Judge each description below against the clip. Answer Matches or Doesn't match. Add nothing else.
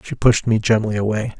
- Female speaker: Doesn't match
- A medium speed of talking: Doesn't match